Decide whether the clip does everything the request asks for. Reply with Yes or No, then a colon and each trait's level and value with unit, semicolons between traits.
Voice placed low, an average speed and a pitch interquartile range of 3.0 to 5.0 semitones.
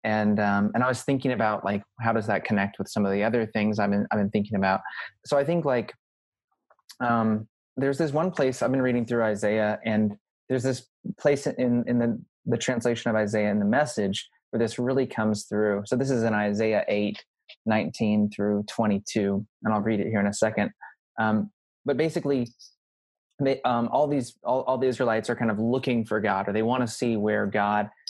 No: low, 110 Hz; fast, 210 wpm; average, 3.4 semitones